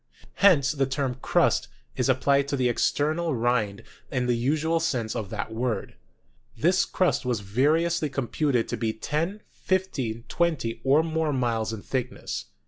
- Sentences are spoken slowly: No, average, 160 wpm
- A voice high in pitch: No, low, 135 Hz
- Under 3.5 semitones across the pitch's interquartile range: No, average, 5.1 semitones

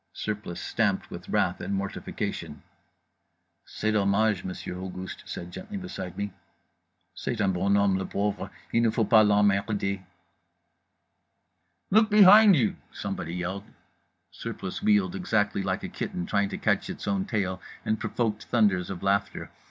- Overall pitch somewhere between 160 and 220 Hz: No, low, 100 Hz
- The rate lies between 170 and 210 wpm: No, average, 150 wpm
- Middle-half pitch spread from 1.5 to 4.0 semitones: Yes, average, 2.7 semitones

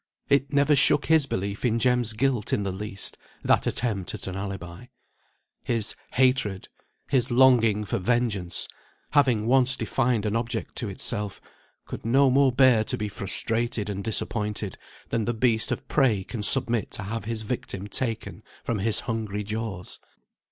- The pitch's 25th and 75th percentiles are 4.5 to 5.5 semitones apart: No, average, 3.4 semitones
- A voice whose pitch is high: No, low, 115 Hz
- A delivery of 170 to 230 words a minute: No, average, 160 wpm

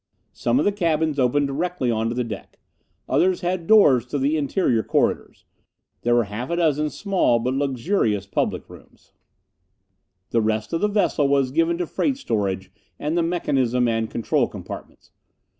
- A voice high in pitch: No, medium, 140 Hz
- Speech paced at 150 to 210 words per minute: Yes, average, 160 wpm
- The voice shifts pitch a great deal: Yes, wide, 6.3 semitones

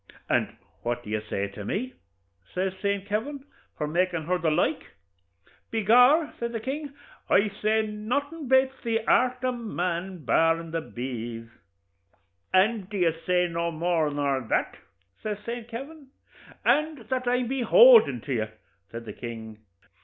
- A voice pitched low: No, high, 200 Hz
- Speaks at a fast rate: No, average, 155 wpm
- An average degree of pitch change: No, wide, 7.8 semitones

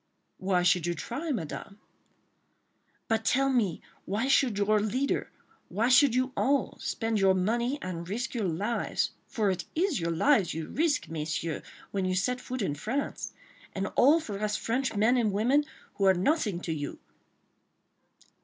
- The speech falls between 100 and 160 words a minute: Yes, average, 150 wpm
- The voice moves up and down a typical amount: No, wide, 5.7 semitones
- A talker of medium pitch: No, high, 215 Hz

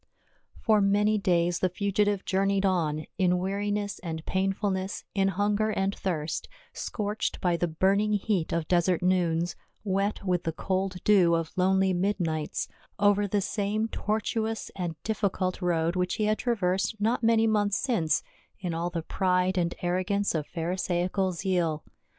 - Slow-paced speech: No, average, 150 wpm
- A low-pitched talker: No, high, 190 Hz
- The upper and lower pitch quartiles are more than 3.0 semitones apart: No, narrow, 2.6 semitones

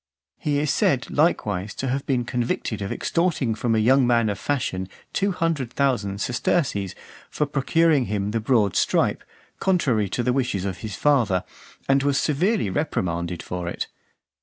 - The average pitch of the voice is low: Yes, low, 125 Hz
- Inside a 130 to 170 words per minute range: Yes, average, 160 wpm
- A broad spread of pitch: Yes, wide, 6.0 semitones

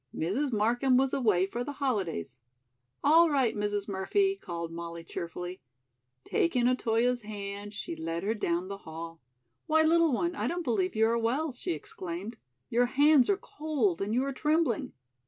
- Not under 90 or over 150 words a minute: No, average, 165 wpm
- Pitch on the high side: Yes, high, 225 Hz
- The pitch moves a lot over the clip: Yes, wide, 6.7 semitones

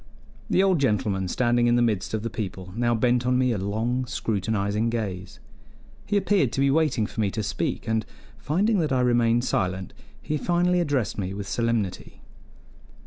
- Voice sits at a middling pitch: No, low, 115 Hz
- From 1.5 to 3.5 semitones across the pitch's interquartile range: No, average, 4.2 semitones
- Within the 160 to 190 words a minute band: Yes, average, 180 wpm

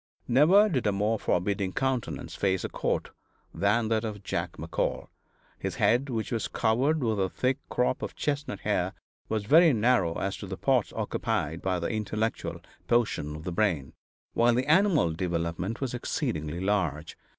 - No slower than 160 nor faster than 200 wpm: Yes, average, 165 wpm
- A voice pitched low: Yes, low, 110 Hz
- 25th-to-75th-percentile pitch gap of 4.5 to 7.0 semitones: Yes, average, 5.3 semitones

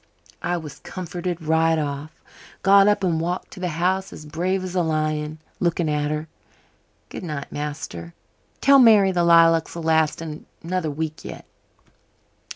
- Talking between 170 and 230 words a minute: No, average, 145 wpm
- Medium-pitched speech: Yes, medium, 165 Hz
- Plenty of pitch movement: No, average, 2.9 semitones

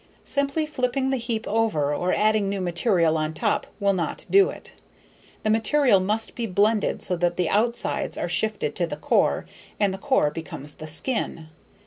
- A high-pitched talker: Yes, high, 210 Hz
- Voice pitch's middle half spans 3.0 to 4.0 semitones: No, wide, 5.4 semitones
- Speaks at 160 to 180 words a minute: Yes, average, 175 wpm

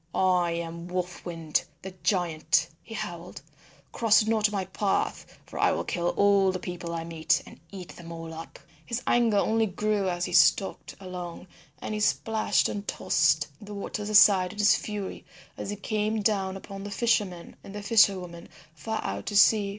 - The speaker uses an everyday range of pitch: Yes, average, 3.2 semitones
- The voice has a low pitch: No, high, 195 Hz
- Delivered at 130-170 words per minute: No, average, 180 wpm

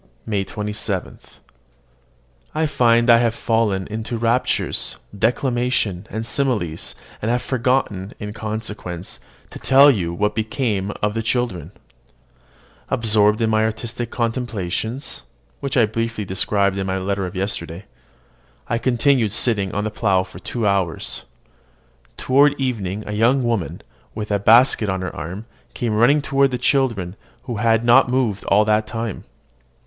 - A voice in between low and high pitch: No, low, 110 Hz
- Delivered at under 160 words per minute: Yes, average, 145 wpm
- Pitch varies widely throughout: No, average, 3.3 semitones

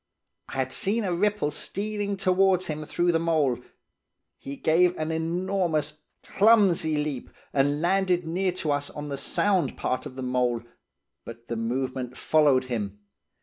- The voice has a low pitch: No, medium, 155 Hz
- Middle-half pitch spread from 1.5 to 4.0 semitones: No, wide, 5.6 semitones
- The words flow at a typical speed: Yes, average, 150 wpm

